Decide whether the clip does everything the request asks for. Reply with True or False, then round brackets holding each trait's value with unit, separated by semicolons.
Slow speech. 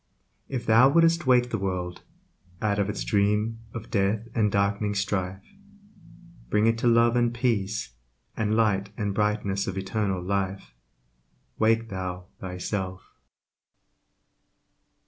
True (125 wpm)